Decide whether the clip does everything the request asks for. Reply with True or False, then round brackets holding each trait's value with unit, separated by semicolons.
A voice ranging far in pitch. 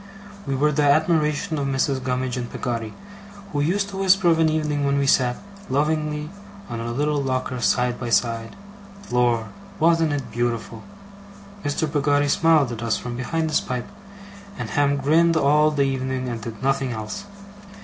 False (3.6 semitones)